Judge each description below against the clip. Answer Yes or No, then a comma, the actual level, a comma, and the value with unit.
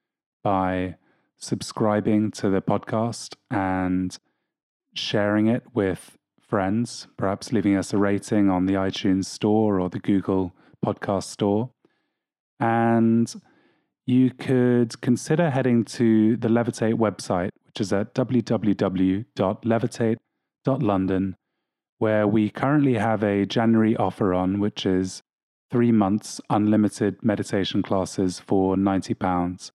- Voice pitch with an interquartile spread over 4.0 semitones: No, average, 3.2 semitones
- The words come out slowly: Yes, slow, 110 wpm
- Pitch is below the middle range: Yes, low, 105 Hz